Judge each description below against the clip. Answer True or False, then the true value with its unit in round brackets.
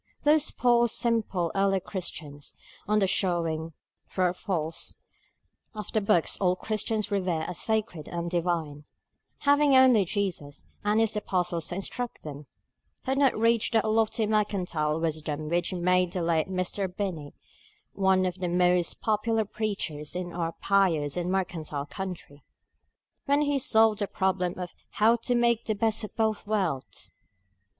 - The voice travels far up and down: False (4.3 semitones)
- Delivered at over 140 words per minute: True (150 wpm)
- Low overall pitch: False (190 Hz)